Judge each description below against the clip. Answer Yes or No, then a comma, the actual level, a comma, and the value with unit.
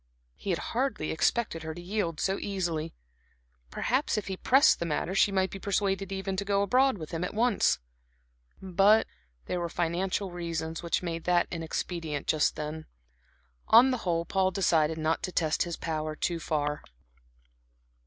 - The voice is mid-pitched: Yes, medium, 175 Hz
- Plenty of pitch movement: No, average, 3.4 semitones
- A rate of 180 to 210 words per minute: No, average, 165 wpm